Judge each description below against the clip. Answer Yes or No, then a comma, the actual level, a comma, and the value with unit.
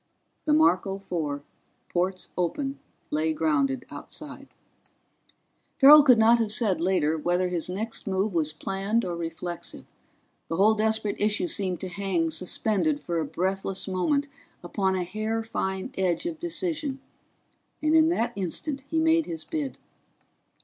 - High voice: Yes, high, 195 Hz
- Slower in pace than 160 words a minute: Yes, average, 140 wpm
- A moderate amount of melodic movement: No, wide, 7.3 semitones